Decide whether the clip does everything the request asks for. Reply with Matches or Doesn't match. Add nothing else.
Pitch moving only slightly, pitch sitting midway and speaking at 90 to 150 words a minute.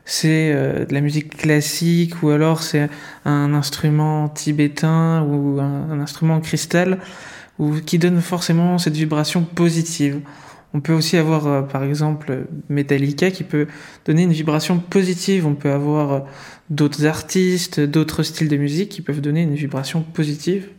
Matches